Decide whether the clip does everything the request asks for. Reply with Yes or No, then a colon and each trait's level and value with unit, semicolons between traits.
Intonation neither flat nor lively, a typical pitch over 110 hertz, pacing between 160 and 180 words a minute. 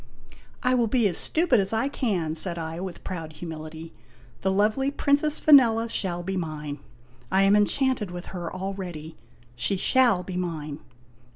No: wide, 5.8 semitones; high, 190 Hz; average, 170 wpm